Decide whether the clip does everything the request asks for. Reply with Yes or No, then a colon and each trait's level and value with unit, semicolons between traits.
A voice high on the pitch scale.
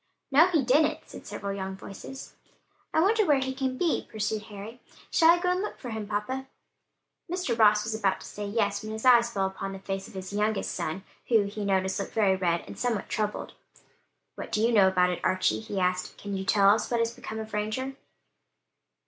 Yes: high, 215 Hz